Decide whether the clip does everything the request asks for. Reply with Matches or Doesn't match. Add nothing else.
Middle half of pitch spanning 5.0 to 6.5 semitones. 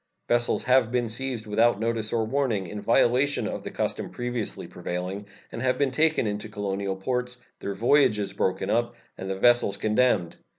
Doesn't match